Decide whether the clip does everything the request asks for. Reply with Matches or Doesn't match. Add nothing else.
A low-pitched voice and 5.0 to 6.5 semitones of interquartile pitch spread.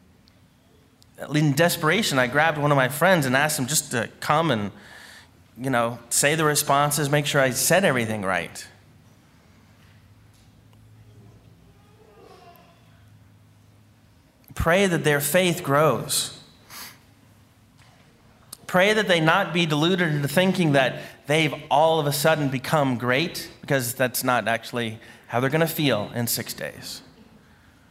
Matches